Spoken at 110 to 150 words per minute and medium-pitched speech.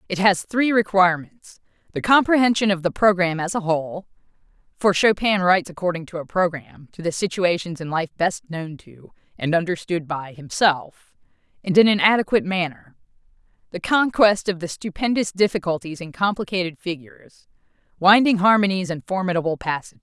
Yes: average, 145 wpm; medium, 180 Hz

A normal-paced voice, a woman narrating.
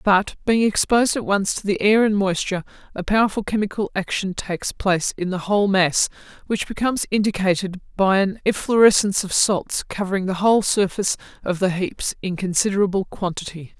Yes: average, 165 wpm; female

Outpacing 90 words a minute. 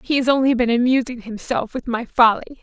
Yes: fast, 205 wpm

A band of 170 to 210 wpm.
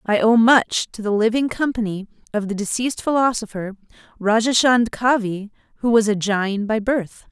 No: average, 155 wpm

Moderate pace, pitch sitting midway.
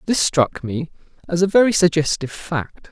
Yes: average, 165 wpm; medium, 165 Hz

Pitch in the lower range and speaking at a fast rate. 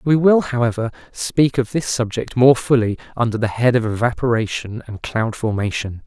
No: low, 120 Hz; average, 170 wpm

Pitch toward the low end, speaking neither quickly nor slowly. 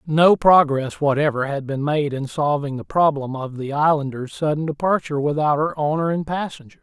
No: medium, 145 Hz; average, 175 wpm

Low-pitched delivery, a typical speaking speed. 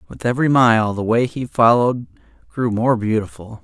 Yes: low, 115 Hz; average, 165 wpm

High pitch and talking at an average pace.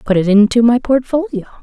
Yes: high, 235 Hz; average, 185 wpm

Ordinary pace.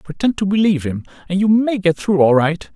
No: fast, 240 wpm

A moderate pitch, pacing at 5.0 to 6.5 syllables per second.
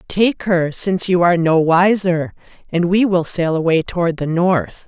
No: medium, 175 Hz; 4.6 syllables/s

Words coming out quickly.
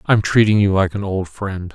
Yes: fast, 275 wpm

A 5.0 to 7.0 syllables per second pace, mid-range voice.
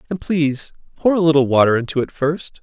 Yes: 5.9 syllables/s; medium, 150 Hz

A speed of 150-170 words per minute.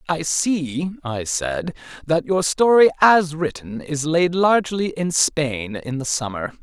Yes: average, 155 wpm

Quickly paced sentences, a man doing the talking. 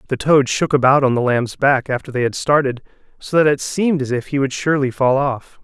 Yes: fast, 245 wpm; male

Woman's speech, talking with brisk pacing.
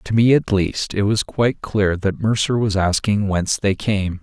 No: male; fast, 215 wpm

